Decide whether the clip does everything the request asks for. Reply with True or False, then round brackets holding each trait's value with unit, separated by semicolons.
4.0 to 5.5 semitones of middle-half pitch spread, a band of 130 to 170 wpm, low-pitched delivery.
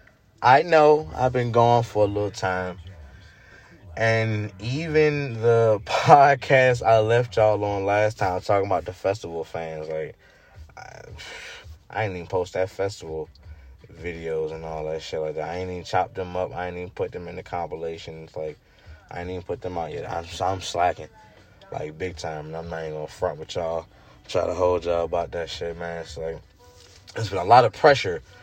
False (4.6 semitones; 195 wpm; 90 Hz)